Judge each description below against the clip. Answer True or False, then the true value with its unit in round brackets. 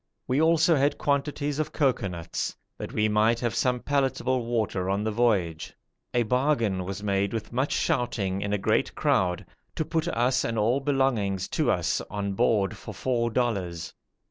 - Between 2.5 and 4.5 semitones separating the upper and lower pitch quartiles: False (5.0 semitones)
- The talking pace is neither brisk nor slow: True (170 wpm)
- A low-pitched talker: True (115 Hz)